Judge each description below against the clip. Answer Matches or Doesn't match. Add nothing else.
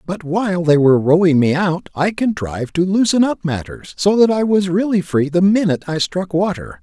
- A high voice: Doesn't match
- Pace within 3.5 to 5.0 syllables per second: Doesn't match